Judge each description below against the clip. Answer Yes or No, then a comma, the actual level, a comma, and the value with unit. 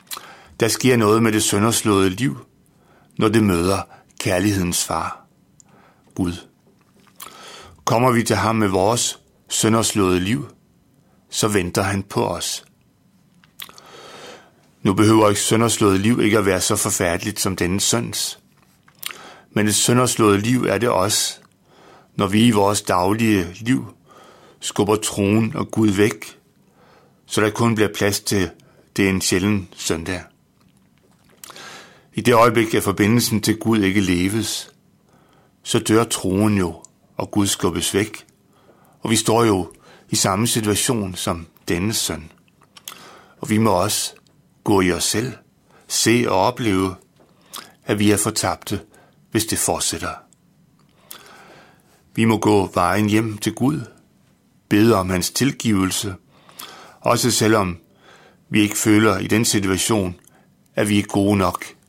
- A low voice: Yes, low, 105 Hz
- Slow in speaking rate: Yes, slow, 130 wpm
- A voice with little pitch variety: Yes, narrow, 2.3 semitones